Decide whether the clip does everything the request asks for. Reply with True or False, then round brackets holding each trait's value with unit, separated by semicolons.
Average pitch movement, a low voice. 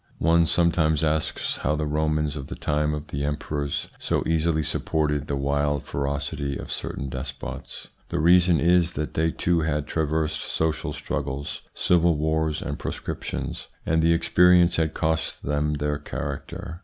False (2.0 semitones; 75 Hz)